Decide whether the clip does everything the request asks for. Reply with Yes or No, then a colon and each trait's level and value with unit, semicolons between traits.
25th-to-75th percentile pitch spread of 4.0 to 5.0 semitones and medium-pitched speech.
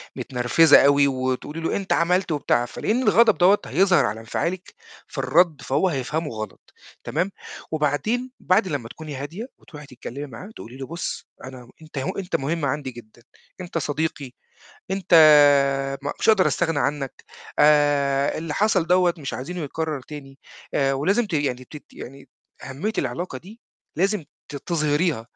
Yes: average, 4.7 semitones; medium, 150 Hz